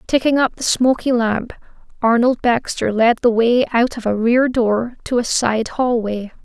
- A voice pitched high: Yes, high, 235 Hz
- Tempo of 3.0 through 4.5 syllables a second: Yes, 4.3 syllables/s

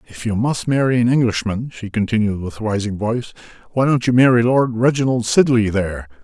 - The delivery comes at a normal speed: Yes, average, 185 wpm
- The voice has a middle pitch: No, low, 115 Hz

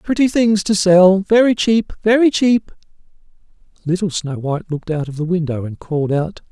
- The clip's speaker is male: Yes, male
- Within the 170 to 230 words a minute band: Yes, average, 175 wpm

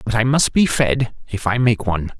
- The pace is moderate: No, fast, 245 wpm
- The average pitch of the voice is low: Yes, low, 115 Hz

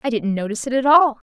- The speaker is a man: No, female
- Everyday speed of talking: No, fast, 275 wpm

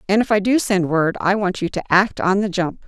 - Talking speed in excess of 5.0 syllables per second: Yes, 5.5 syllables/s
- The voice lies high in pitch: Yes, high, 195 Hz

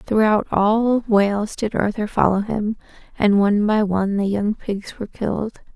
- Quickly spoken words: No, average, 165 wpm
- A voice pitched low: No, high, 210 Hz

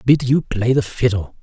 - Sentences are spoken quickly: Yes, fast, 210 wpm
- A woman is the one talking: No, male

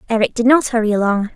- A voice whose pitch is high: Yes, high, 225 Hz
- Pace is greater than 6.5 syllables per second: Yes, 6.8 syllables/s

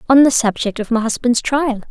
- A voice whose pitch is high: Yes, high, 245 Hz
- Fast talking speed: Yes, fast, 220 wpm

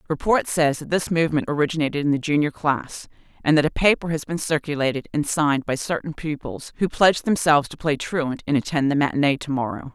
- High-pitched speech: No, medium, 150 Hz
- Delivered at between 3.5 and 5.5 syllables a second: No, 6.1 syllables/s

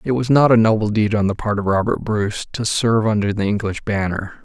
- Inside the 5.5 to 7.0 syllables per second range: Yes, 5.9 syllables/s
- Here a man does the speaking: Yes, male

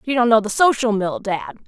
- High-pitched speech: Yes, high, 225 Hz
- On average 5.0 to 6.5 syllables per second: Yes, 5.5 syllables/s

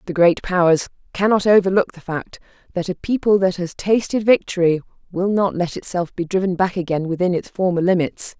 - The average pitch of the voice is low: No, medium, 185 Hz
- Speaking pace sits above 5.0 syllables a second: Yes, 5.5 syllables/s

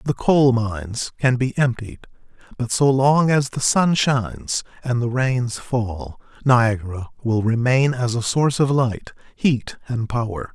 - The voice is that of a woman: No, male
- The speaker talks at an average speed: Yes, average, 160 wpm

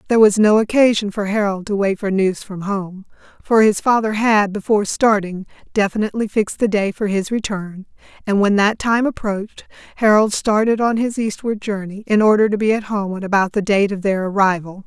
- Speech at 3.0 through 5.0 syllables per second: No, 5.4 syllables/s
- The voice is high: Yes, high, 205 Hz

